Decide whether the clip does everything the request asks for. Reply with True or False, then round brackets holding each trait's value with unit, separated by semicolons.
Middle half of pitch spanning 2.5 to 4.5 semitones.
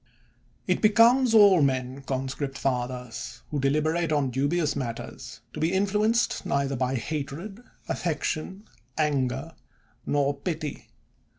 False (4.9 semitones)